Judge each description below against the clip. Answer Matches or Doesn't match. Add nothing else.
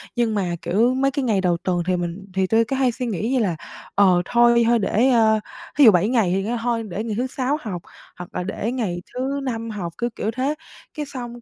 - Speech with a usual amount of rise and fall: Matches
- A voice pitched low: Doesn't match